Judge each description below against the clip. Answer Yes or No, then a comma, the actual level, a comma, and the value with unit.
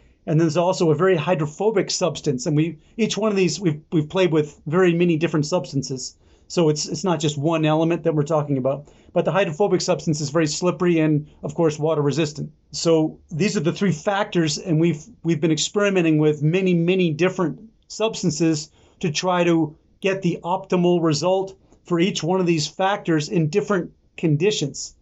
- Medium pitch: Yes, medium, 170 Hz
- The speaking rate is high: No, average, 185 wpm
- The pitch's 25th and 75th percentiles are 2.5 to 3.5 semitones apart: Yes, average, 2.9 semitones